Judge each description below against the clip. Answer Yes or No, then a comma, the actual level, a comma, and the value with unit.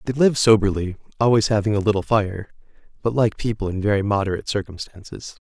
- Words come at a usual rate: Yes, average, 165 wpm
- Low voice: Yes, low, 105 Hz